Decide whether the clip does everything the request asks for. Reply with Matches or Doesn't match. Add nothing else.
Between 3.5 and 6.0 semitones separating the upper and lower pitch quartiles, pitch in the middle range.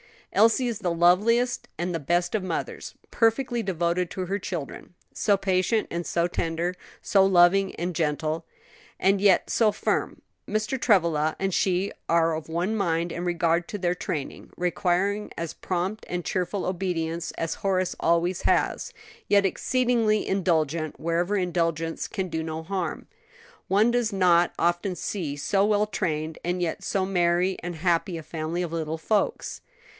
Doesn't match